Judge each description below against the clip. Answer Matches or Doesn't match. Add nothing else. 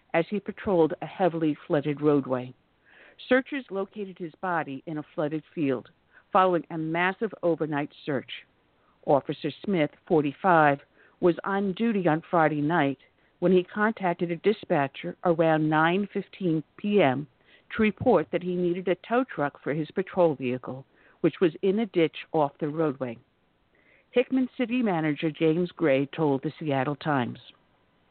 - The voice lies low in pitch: Doesn't match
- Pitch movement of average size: Matches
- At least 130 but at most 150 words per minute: Matches